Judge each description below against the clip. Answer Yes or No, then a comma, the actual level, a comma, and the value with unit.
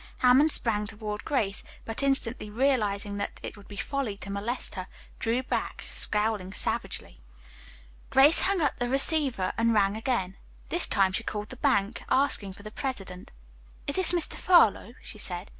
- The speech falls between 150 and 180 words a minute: Yes, average, 165 wpm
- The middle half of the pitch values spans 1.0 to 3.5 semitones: No, average, 4.9 semitones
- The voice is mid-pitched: No, high, 220 Hz